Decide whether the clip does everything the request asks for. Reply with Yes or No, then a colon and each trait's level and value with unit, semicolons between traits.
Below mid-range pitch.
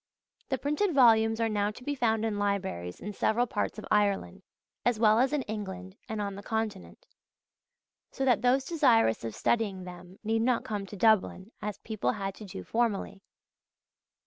No: high, 215 Hz